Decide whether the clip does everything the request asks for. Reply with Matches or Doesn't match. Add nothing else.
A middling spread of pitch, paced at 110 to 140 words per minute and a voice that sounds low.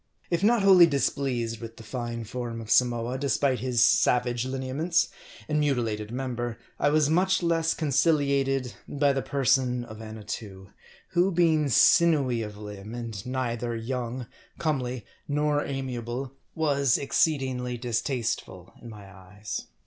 Matches